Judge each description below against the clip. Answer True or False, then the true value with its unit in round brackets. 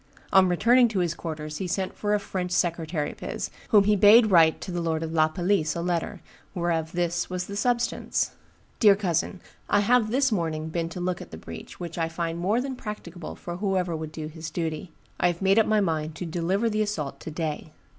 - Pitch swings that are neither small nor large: True (3.8 semitones)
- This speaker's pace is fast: True (220 wpm)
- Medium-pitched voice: True (175 Hz)